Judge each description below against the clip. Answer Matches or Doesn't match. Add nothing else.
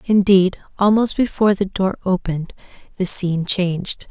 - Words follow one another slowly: Matches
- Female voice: Matches